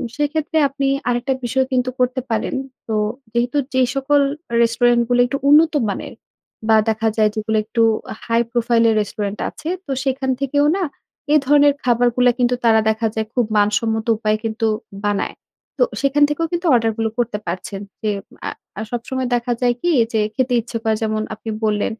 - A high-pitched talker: Yes, high, 240 Hz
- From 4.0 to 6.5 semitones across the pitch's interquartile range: No, average, 3.2 semitones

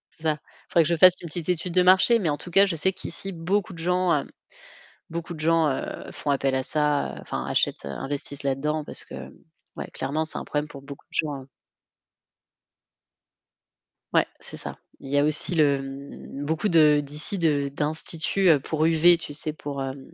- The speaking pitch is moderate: Yes, medium, 155 Hz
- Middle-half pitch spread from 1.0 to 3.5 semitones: Yes, average, 3.1 semitones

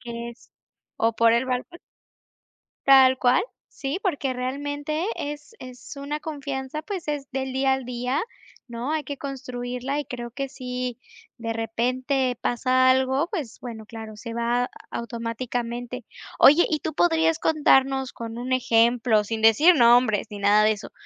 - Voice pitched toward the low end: No, very high, 255 Hz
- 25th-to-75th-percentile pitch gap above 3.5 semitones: No, average, 3.0 semitones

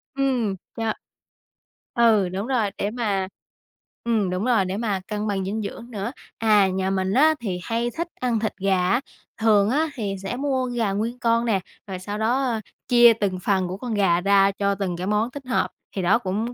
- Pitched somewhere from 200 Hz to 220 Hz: Yes, high, 210 Hz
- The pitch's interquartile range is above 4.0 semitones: No, average, 3.4 semitones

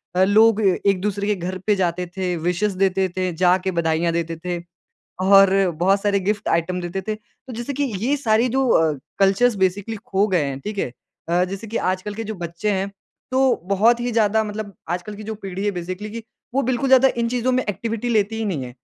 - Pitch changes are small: No, average, 3.3 semitones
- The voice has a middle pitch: No, high, 200 Hz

